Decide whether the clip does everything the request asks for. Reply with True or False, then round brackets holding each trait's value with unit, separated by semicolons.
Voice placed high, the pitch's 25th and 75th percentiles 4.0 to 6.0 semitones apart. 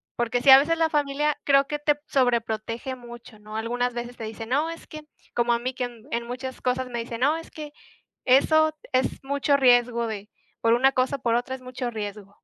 False (250 Hz; 2.9 semitones)